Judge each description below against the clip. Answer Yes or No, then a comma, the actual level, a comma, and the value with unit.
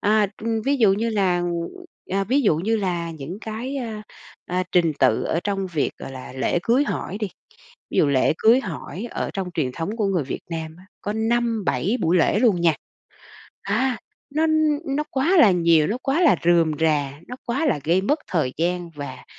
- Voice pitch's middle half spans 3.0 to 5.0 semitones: No, wide, 5.6 semitones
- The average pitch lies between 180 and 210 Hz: Yes, high, 195 Hz